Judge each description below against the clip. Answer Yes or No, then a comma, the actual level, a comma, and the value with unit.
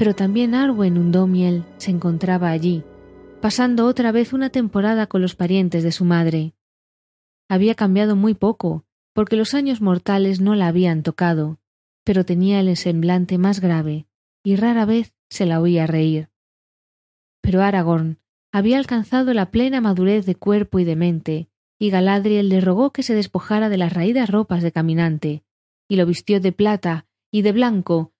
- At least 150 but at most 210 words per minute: Yes, average, 160 wpm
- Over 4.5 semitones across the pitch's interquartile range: No, average, 4.0 semitones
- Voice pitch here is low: No, medium, 185 Hz